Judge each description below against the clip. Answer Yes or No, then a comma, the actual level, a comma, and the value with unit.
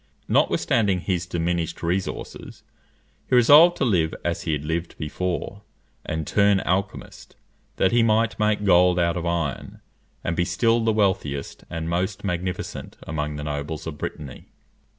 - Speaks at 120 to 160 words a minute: Yes, average, 150 wpm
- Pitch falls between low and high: No, very low, 90 Hz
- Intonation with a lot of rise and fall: No, average, 3.9 semitones